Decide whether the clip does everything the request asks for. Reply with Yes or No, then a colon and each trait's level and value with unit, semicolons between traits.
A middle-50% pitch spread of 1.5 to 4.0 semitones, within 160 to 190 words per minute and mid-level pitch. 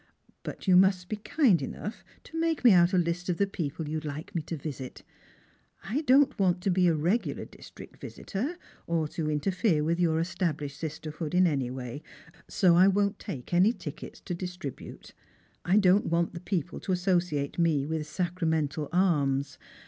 Yes: average, 3.7 semitones; average, 175 wpm; medium, 175 Hz